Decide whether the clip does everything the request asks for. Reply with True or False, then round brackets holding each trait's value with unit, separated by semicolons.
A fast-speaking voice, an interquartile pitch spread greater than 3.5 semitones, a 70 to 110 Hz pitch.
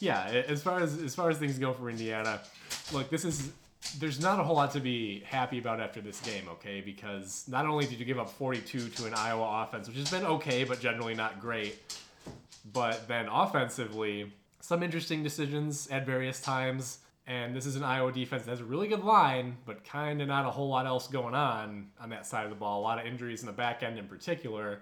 False (225 wpm; 4.2 semitones; 125 Hz)